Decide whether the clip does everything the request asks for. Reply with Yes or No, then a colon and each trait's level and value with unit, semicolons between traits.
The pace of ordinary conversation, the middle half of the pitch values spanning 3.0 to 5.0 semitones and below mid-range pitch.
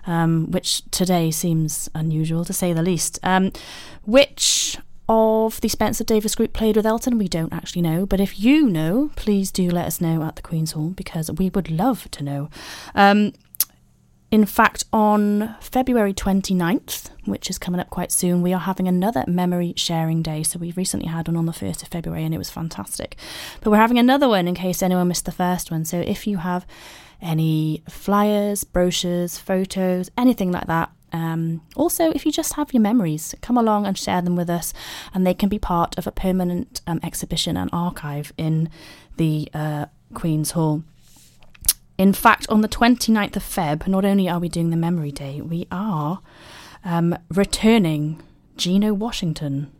No: average, 180 wpm; average, 4.0 semitones; medium, 180 Hz